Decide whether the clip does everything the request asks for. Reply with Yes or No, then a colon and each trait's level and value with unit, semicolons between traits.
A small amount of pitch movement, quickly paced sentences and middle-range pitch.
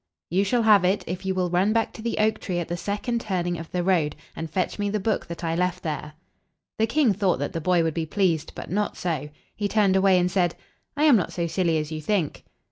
No: average, 3.5 semitones; fast, 255 wpm; medium, 180 Hz